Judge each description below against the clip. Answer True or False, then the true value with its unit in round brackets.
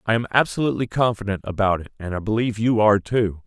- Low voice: True (110 Hz)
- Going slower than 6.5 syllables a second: False (6.9 syllables/s)